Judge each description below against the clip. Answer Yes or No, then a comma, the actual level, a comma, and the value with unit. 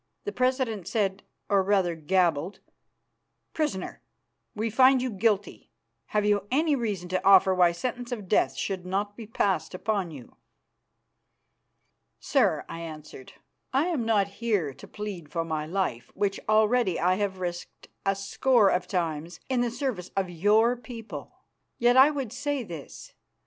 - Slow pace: No, average, 150 wpm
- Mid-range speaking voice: No, high, 200 Hz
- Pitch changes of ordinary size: Yes, average, 4.6 semitones